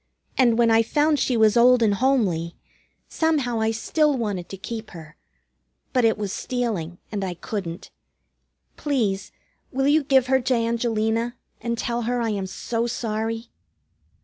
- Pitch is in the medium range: No, high, 230 Hz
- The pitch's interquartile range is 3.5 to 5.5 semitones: No, average, 3.0 semitones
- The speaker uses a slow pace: No, average, 155 wpm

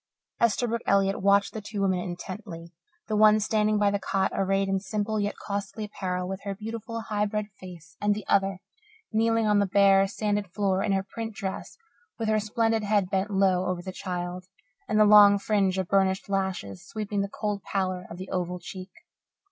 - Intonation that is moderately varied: No, narrow, 2.0 semitones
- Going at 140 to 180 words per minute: No, average, 190 wpm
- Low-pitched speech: No, high, 200 Hz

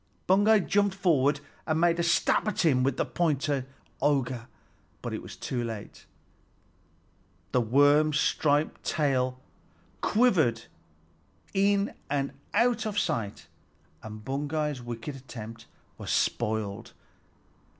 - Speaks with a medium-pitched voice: Yes, medium, 145 Hz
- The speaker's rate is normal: No, slow, 110 wpm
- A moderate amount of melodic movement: No, wide, 6.1 semitones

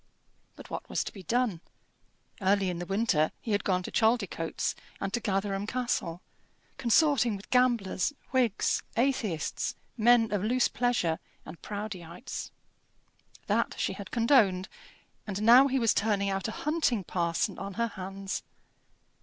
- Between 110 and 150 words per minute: Yes, average, 145 wpm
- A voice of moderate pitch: No, high, 205 Hz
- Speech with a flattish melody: No, average, 4.1 semitones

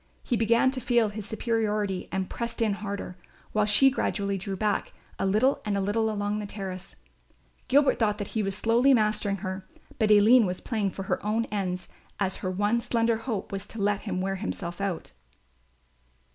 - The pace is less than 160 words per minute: No, average, 185 wpm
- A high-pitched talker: Yes, high, 210 Hz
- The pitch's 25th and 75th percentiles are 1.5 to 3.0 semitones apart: Yes, narrow, 2.5 semitones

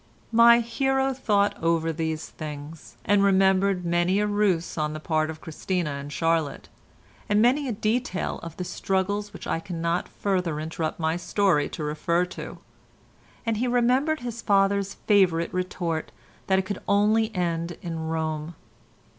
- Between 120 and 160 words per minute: Yes, average, 155 wpm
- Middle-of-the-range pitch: Yes, medium, 180 Hz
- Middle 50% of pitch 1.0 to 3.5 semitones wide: No, average, 4.1 semitones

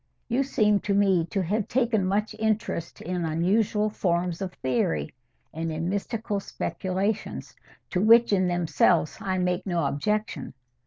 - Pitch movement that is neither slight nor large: Yes, average, 3.7 semitones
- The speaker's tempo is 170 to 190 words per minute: No, average, 145 wpm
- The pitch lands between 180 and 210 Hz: Yes, high, 190 Hz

